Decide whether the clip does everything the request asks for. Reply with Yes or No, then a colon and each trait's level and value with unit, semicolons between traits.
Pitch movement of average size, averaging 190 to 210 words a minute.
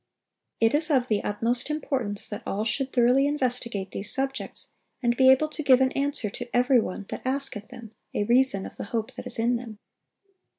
Yes: average, 3.2 semitones; average, 200 wpm